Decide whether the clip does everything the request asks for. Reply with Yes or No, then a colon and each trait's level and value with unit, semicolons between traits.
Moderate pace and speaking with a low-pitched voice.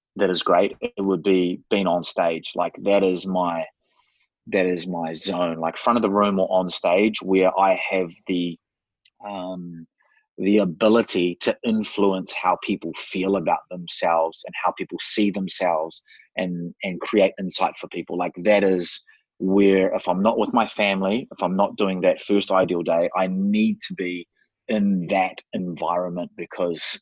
Yes: average, 170 wpm; very low, 95 Hz